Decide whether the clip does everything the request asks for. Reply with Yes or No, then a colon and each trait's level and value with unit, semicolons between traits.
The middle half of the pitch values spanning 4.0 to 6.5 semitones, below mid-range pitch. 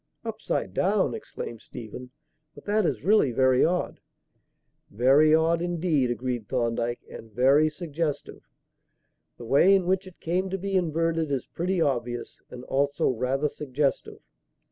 No: average, 5.3 semitones; medium, 145 Hz